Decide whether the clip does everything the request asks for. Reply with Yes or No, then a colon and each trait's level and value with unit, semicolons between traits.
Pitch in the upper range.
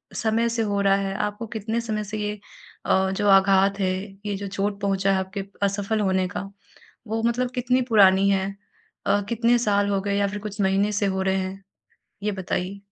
Yes: high, 200 Hz